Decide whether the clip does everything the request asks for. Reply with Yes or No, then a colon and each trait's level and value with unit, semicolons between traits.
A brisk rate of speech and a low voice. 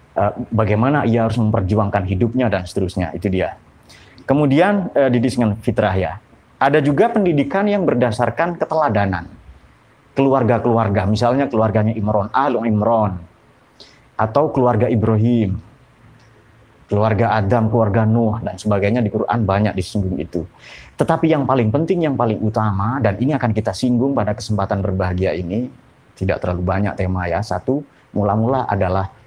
No: average, 130 wpm; low, 110 Hz